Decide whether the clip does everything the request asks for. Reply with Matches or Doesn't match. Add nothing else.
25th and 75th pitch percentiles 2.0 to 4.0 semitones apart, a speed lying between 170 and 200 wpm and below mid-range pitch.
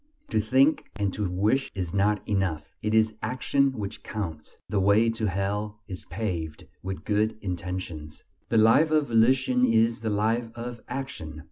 Doesn't match